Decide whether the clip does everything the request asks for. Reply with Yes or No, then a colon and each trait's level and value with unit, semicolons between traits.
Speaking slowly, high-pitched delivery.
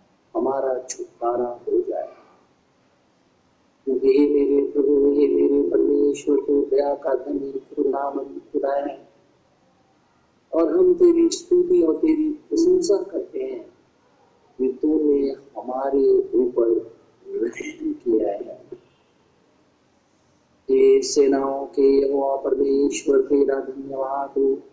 Yes: slow, 95 wpm; very high, 310 Hz